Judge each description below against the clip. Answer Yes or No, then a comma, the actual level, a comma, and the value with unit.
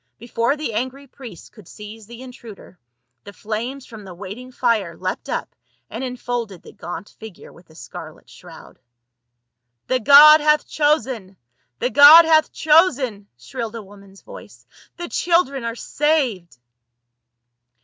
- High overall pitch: Yes, high, 235 Hz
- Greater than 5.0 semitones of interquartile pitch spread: Yes, wide, 5.5 semitones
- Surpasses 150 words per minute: No, average, 140 wpm